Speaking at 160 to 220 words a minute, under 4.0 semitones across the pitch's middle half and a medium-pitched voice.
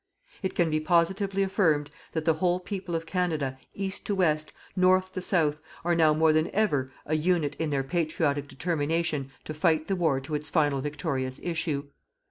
Yes: average, 180 wpm; average, 3.4 semitones; medium, 160 Hz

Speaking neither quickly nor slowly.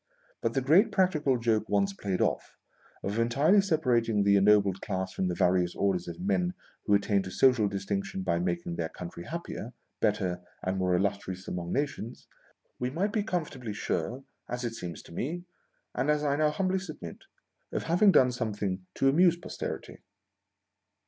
Yes: average, 175 wpm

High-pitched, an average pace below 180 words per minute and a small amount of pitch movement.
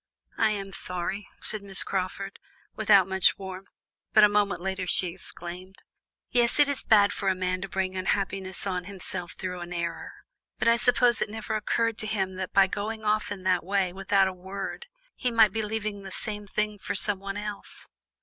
No: high, 195 Hz; average, 190 wpm; narrow, 2.1 semitones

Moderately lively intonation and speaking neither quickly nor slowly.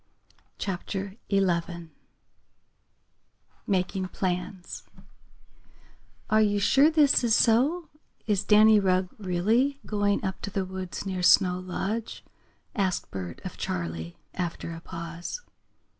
No: average, 3.2 semitones; slow, 110 wpm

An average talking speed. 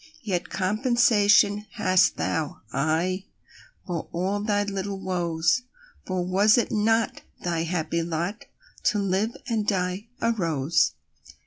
No: slow, 100 wpm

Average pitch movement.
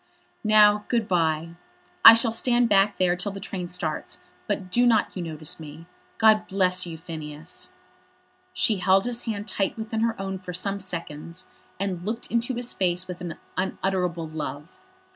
Yes: average, 4.0 semitones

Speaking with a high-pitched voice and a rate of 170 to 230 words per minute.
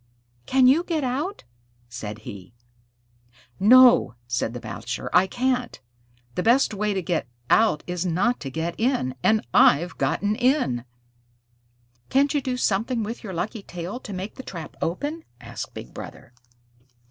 No: high, 210 Hz; average, 150 wpm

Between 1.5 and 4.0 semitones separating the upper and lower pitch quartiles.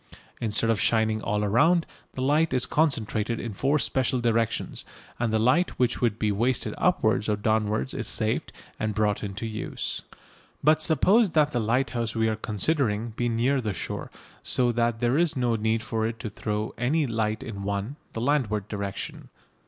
Yes: average, 3.2 semitones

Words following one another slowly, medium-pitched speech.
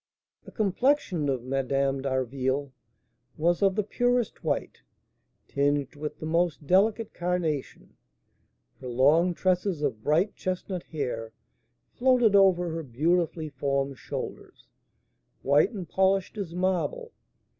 Yes: slow, 115 wpm; medium, 165 Hz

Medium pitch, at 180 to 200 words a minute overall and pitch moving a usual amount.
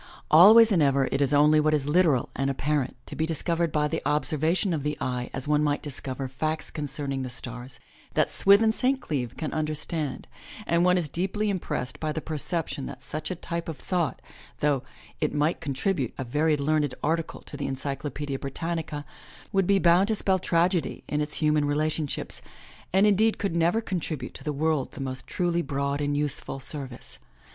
Yes: medium, 150 Hz; average, 185 wpm; average, 3.3 semitones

